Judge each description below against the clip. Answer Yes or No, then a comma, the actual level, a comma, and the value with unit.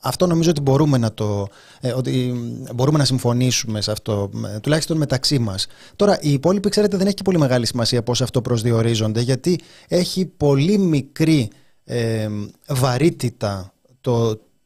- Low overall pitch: Yes, low, 130 Hz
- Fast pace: No, average, 145 wpm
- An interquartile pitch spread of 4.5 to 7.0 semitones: Yes, average, 5.1 semitones